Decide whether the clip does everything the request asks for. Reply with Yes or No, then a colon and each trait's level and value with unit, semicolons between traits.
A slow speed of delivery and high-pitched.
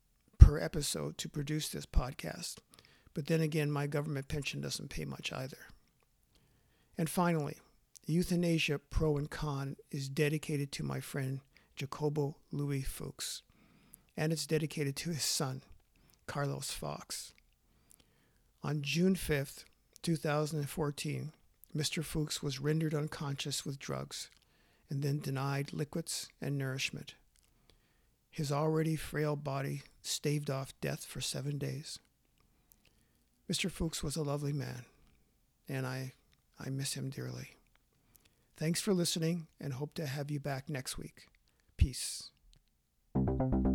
No: slow, 120 wpm; medium, 145 Hz